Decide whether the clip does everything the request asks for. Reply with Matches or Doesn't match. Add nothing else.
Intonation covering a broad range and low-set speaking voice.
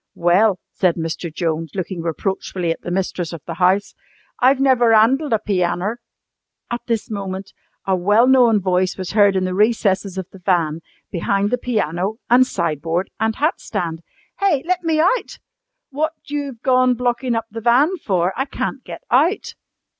Doesn't match